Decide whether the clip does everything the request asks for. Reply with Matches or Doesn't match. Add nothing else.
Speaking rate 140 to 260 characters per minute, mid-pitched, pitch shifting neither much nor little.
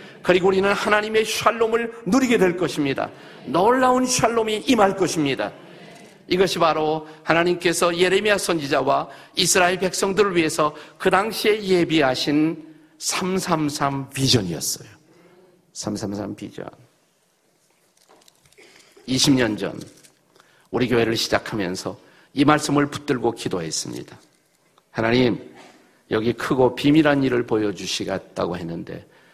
Doesn't match